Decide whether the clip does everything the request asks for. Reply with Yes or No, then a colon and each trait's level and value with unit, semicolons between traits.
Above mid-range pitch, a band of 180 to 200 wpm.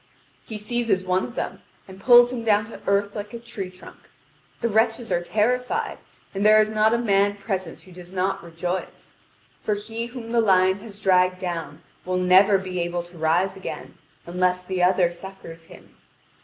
Yes: high, 195 Hz; average, 185 wpm